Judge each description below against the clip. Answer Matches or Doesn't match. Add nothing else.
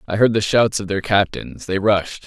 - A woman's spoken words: Doesn't match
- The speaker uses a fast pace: Matches